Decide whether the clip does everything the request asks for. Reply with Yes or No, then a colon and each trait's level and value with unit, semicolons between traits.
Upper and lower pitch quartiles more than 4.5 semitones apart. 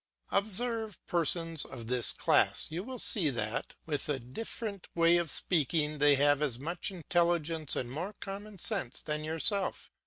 Yes: average, 5.1 semitones